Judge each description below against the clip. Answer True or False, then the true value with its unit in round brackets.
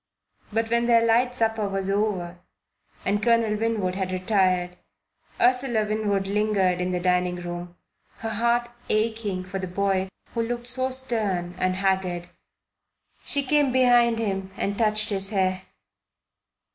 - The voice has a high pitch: True (205 Hz)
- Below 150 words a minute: True (140 wpm)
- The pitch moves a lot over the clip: False (3.7 semitones)